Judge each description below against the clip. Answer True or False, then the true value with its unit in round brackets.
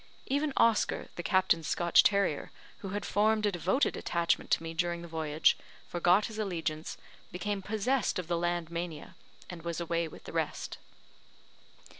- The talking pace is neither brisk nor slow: True (160 wpm)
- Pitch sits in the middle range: True (175 Hz)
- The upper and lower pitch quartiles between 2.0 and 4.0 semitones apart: True (3.5 semitones)